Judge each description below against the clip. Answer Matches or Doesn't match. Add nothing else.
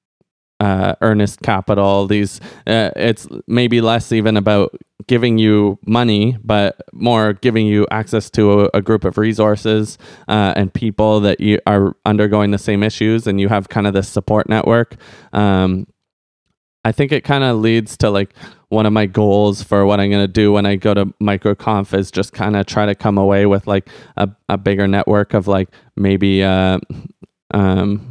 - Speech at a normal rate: Matches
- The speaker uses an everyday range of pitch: Doesn't match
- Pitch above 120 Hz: Doesn't match